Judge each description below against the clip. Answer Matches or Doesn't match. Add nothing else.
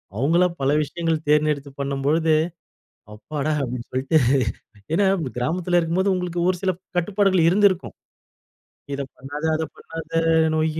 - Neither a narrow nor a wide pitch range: Matches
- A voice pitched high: Doesn't match